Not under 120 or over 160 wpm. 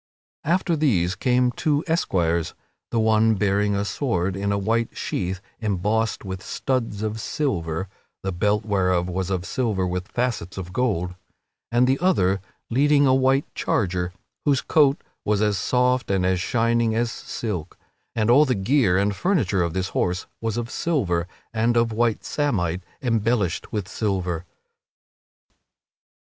Yes: average, 150 wpm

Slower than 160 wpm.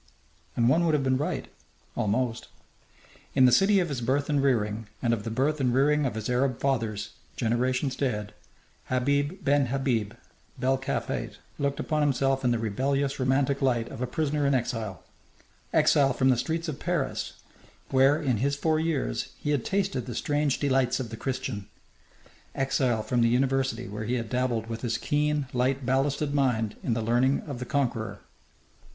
No: average, 175 wpm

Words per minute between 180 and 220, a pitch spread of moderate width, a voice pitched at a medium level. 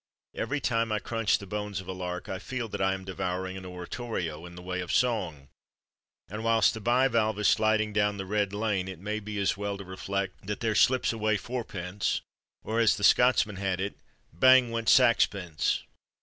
No: average, 195 wpm; average, 3.2 semitones; low, 105 Hz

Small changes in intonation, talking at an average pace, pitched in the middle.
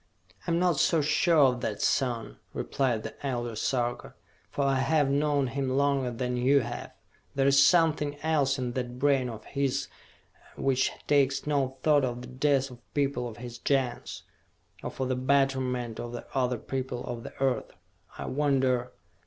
No: narrow, 2.2 semitones; average, 170 wpm; low, 130 Hz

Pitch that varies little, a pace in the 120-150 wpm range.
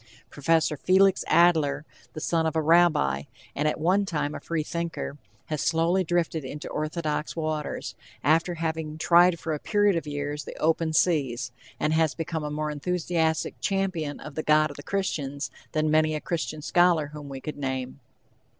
No: narrow, 2.1 semitones; average, 170 wpm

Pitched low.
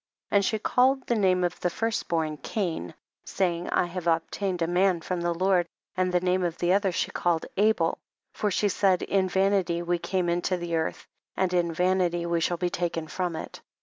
No: medium, 180 Hz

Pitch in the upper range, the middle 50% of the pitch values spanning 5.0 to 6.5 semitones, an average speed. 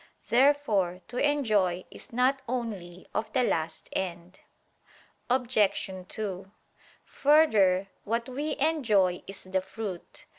No: high, 215 Hz; wide, 5.5 semitones; slow, 110 wpm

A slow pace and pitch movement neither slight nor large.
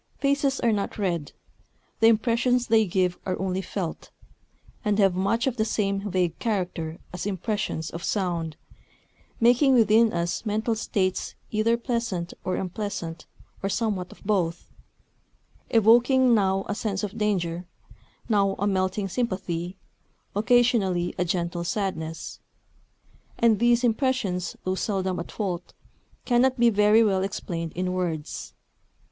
Yes: slow, 130 wpm; average, 4.0 semitones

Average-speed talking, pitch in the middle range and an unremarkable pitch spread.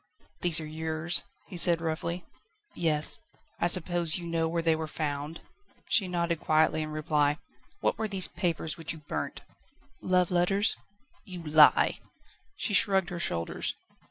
No: average, 150 wpm; medium, 165 Hz; narrow, 2.1 semitones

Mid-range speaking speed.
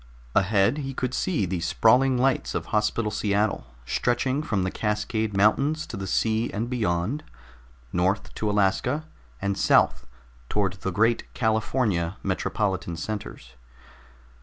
No: slow, 130 wpm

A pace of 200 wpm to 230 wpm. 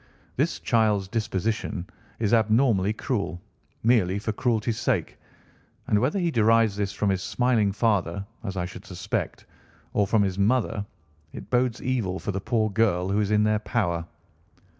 No: average, 160 wpm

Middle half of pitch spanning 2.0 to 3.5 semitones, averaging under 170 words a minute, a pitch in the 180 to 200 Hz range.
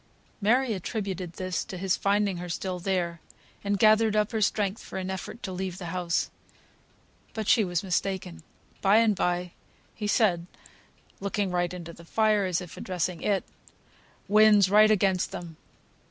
Yes: average, 2.8 semitones; average, 160 wpm; high, 190 Hz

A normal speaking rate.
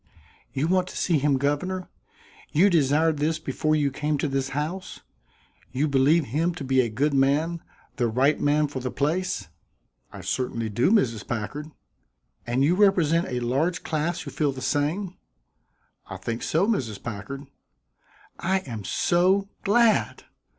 Yes: average, 155 wpm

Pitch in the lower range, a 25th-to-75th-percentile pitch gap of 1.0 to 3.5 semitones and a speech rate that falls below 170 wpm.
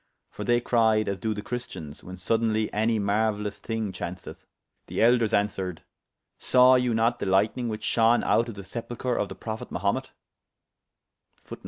Yes: low, 110 Hz; narrow, 2.6 semitones; average, 160 wpm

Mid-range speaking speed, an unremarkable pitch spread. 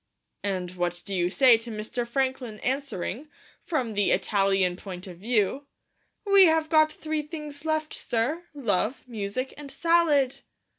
No: average, 145 wpm; wide, 7.0 semitones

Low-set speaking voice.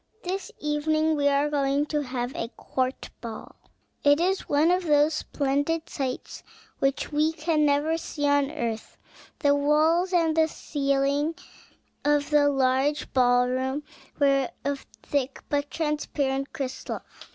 No: very high, 285 Hz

